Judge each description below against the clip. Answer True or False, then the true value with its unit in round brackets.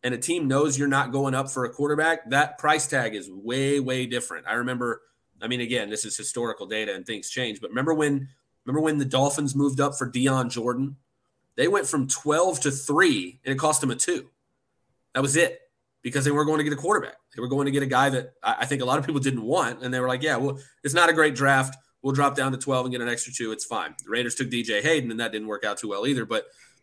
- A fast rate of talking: True (265 wpm)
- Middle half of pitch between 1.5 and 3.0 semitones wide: True (2.6 semitones)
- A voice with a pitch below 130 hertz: False (135 Hz)